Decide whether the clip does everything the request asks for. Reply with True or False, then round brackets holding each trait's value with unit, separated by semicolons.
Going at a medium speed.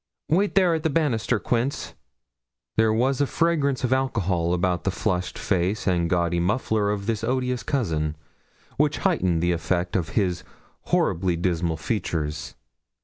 True (145 wpm)